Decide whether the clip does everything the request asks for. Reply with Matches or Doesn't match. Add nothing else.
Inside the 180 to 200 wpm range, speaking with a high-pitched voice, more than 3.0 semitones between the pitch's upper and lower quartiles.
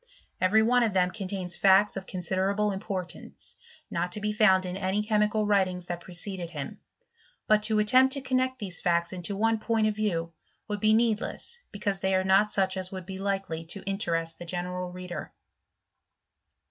Doesn't match